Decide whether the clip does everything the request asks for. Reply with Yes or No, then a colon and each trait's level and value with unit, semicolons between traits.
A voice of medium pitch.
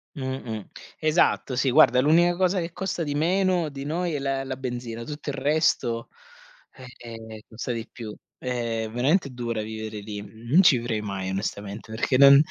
No: low, 130 Hz